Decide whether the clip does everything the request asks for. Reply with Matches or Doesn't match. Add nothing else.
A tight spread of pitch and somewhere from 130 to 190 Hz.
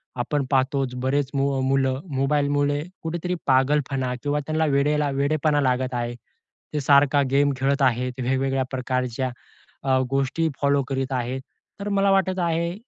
Matches